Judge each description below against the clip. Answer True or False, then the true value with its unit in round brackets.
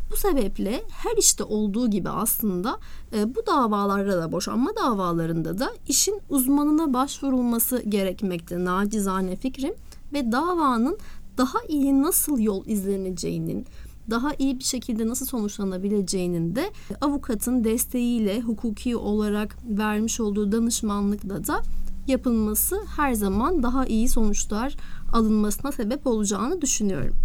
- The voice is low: False (230 Hz)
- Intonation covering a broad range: False (4.8 semitones)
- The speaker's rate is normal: True (110 wpm)